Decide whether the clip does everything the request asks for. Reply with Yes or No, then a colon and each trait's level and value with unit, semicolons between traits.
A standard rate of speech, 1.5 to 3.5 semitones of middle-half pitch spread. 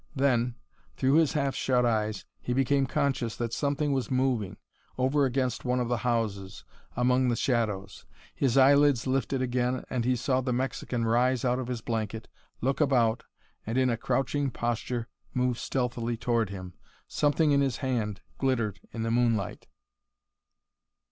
Yes: average, 155 wpm; narrow, 2.4 semitones